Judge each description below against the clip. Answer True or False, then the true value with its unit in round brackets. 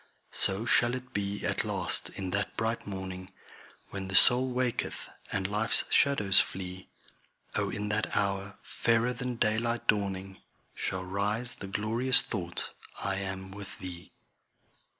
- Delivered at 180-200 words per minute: False (140 wpm)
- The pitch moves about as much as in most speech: True (3.3 semitones)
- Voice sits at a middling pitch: False (100 Hz)